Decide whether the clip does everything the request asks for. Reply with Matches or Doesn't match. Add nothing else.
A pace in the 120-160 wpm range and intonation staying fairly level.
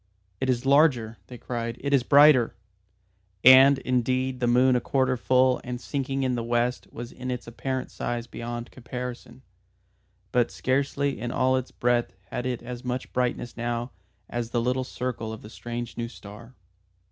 Doesn't match